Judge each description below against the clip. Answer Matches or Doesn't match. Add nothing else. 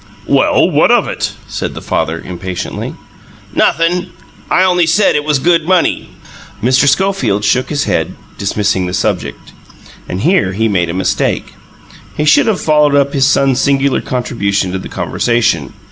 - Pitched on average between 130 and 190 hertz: Matches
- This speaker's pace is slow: Doesn't match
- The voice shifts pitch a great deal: Matches